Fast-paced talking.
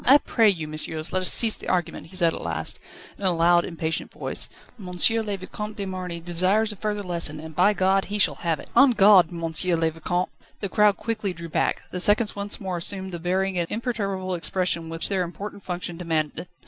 Yes: fast, 210 wpm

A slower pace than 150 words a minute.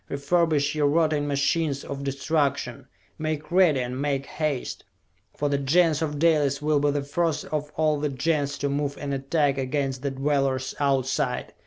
No: average, 165 wpm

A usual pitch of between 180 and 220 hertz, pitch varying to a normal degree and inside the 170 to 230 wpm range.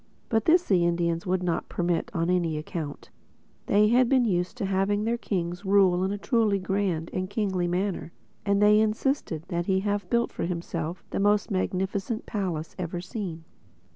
Yes: high, 190 Hz; average, 3.1 semitones; average, 175 wpm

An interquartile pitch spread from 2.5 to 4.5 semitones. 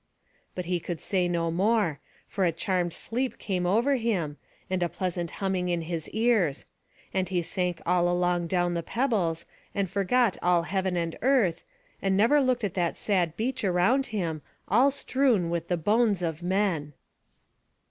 Yes: average, 3.9 semitones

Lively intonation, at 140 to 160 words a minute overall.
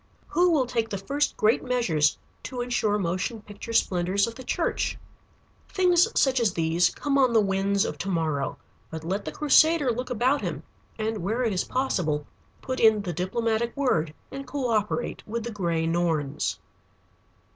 No: wide, 5.8 semitones; average, 170 wpm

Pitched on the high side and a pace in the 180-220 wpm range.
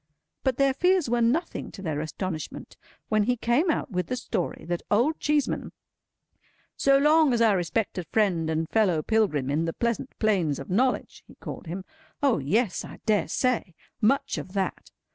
No: high, 220 Hz; average, 165 wpm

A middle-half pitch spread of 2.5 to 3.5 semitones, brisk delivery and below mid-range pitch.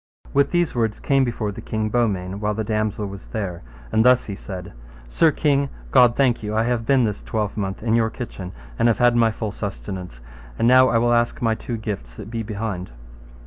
Yes: average, 2.9 semitones; fast, 210 wpm; low, 110 Hz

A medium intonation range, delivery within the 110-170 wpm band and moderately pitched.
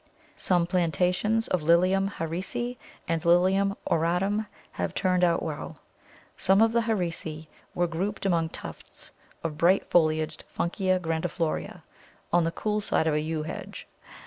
Yes: average, 3.0 semitones; average, 145 wpm; medium, 175 Hz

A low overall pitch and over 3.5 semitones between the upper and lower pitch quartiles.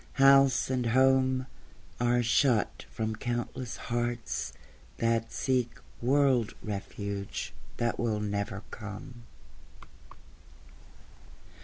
No: low, 120 Hz; average, 2.9 semitones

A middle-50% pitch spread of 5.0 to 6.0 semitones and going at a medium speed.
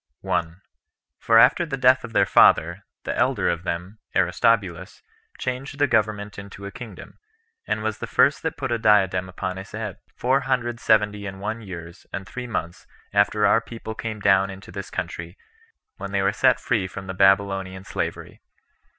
No: average, 3.4 semitones; average, 175 wpm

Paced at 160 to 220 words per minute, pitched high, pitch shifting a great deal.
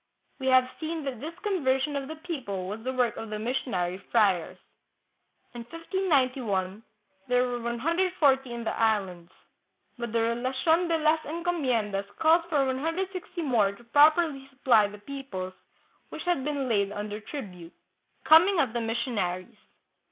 No: average, 150 wpm; very high, 255 Hz; wide, 6.4 semitones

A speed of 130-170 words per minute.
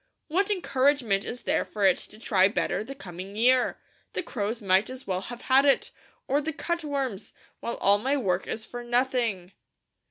No: average, 180 wpm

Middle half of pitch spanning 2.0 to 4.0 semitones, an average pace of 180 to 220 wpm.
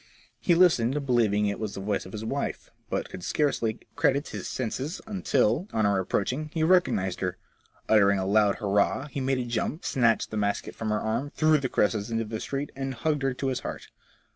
No: average, 5.0 semitones; fast, 205 wpm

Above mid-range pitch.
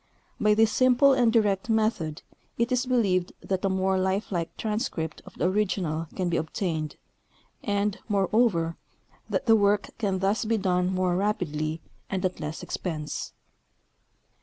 Yes: high, 195 Hz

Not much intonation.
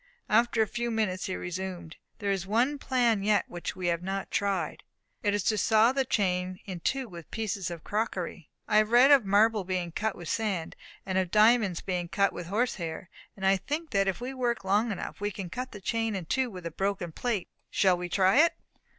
No: average, 3.8 semitones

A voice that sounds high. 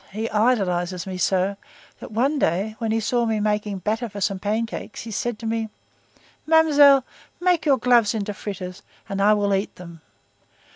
Yes: high, 215 Hz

